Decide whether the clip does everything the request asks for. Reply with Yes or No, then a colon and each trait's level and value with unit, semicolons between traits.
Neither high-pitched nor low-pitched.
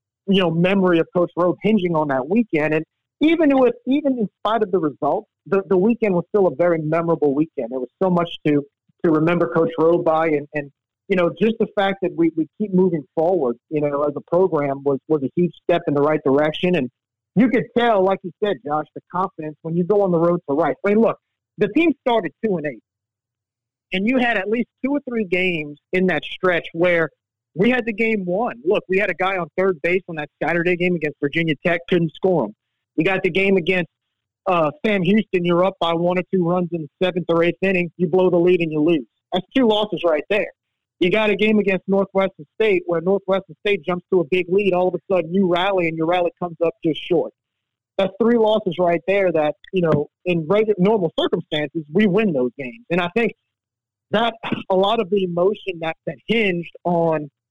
Yes: medium, 175 Hz